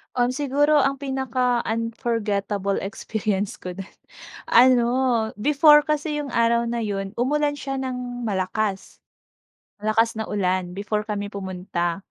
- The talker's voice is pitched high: Yes, high, 230 Hz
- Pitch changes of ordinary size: Yes, average, 4.6 semitones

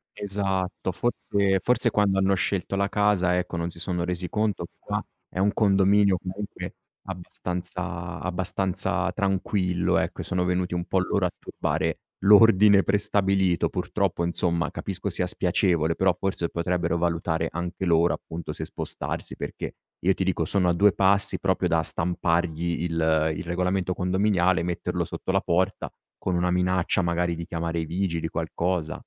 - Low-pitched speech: Yes, very low, 90 Hz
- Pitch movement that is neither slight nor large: No, narrow, 2.1 semitones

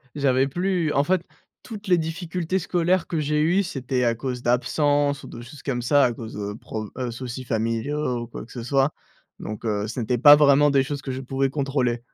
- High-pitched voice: No, low, 135 Hz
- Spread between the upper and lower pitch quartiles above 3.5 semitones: Yes, average, 3.9 semitones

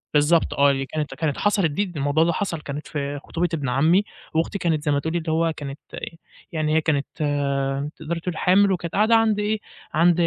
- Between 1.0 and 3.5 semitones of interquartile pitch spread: Yes, average, 3.2 semitones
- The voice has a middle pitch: Yes, medium, 160 Hz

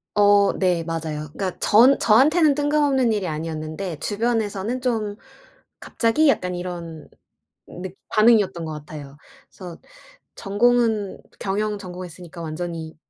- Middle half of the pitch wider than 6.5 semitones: No, average, 5.3 semitones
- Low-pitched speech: No, high, 195 Hz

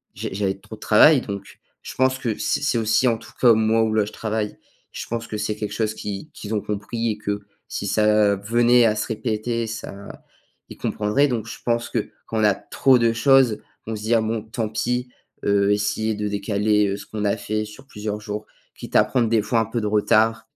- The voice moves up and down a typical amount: No, narrow, 1.7 semitones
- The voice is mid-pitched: No, low, 110 Hz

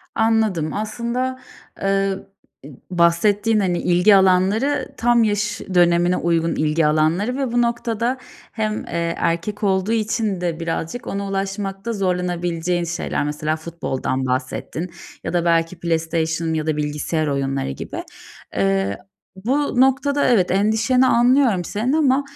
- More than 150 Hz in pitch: Yes, high, 190 Hz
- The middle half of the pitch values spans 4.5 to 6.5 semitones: Yes, average, 5.2 semitones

